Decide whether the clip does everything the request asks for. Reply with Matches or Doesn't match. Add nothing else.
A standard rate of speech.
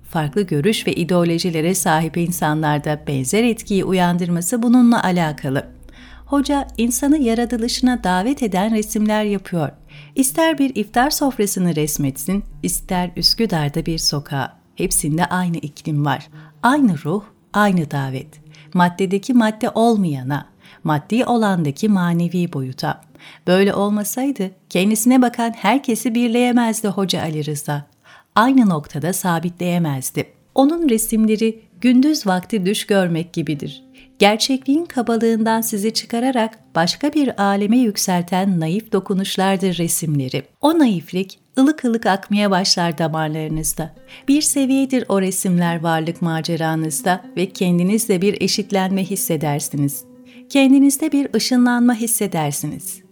Matches